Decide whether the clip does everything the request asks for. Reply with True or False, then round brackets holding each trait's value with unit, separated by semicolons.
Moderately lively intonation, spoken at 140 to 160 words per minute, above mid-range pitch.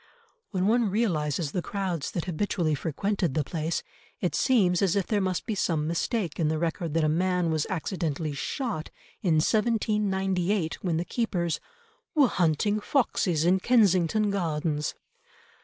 False (4.2 semitones; 150 wpm; 180 Hz)